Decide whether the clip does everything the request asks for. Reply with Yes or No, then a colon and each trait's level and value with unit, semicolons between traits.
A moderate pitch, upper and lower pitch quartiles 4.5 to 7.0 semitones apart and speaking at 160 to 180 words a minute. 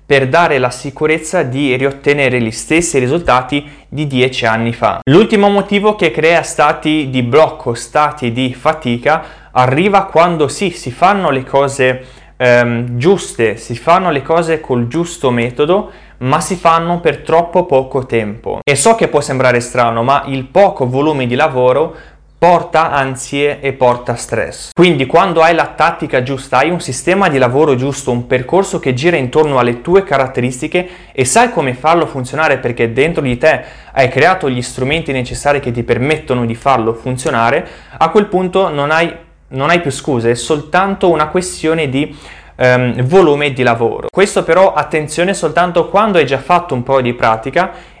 Yes: medium, 145 Hz; average, 4.9 semitones; average, 165 wpm